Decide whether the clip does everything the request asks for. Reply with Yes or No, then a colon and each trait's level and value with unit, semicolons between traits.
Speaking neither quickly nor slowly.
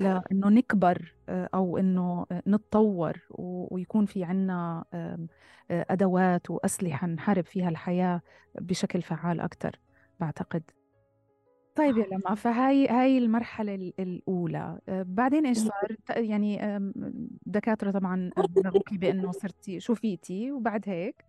Yes: average, 100 wpm